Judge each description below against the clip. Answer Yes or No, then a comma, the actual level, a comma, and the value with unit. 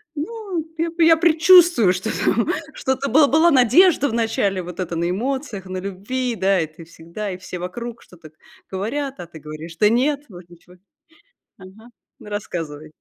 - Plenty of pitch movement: Yes, wide, 7.9 semitones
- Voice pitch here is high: Yes, high, 215 Hz